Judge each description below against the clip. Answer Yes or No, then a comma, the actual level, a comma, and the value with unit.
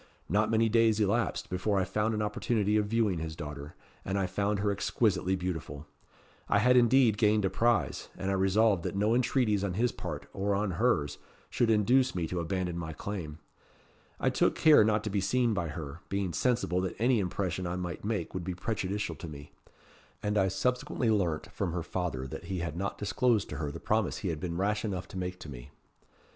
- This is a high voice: No, low, 100 Hz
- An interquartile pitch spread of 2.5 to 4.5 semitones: Yes, average, 3.5 semitones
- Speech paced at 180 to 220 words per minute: Yes, fast, 205 wpm